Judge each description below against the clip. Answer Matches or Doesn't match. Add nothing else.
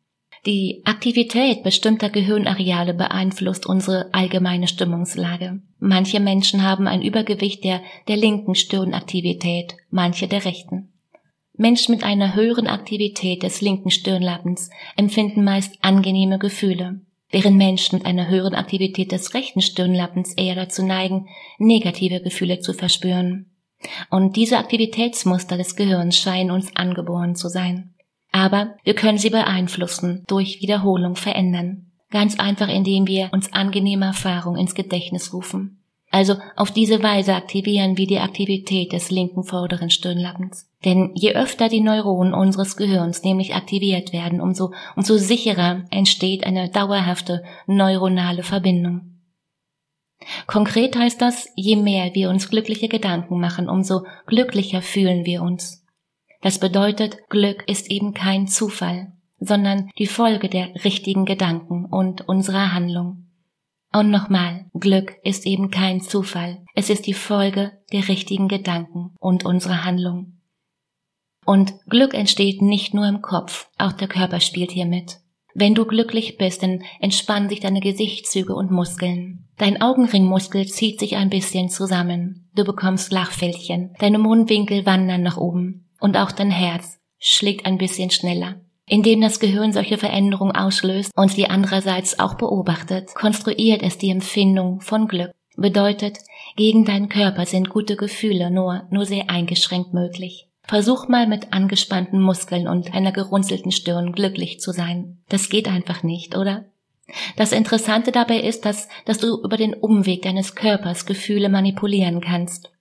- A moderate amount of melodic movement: Doesn't match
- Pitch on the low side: Doesn't match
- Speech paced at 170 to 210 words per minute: Doesn't match